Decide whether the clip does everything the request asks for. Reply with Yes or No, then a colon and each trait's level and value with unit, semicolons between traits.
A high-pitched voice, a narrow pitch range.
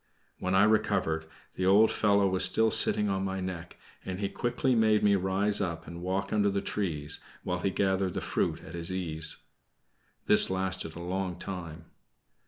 No: very low, 95 Hz; narrow, 2.3 semitones